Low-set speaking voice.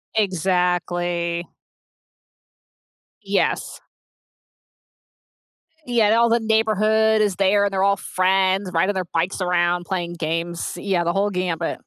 No: medium, 185 Hz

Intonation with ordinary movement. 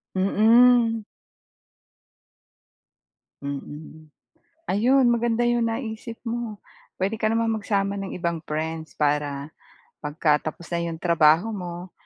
No: wide, 6.2 semitones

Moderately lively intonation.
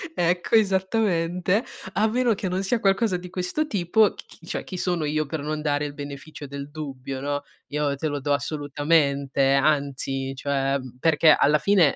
Yes: average, 4.4 semitones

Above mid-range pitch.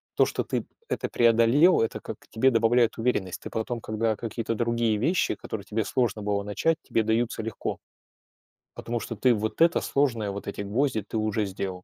No: low, 115 Hz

